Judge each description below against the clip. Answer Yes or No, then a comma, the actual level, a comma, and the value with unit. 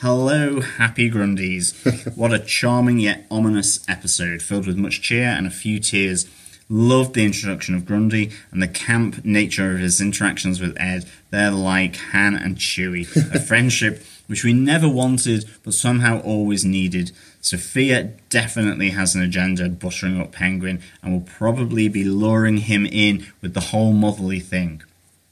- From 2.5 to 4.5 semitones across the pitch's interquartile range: Yes, average, 3.4 semitones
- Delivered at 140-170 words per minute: Yes, average, 155 wpm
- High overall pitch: No, low, 100 Hz